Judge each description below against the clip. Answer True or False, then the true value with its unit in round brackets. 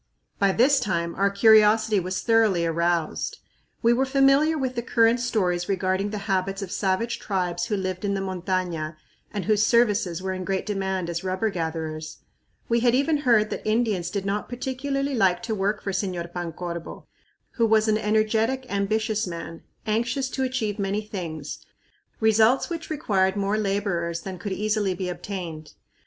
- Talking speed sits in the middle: True (165 wpm)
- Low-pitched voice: False (200 Hz)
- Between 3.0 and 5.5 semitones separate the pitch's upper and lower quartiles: True (3.6 semitones)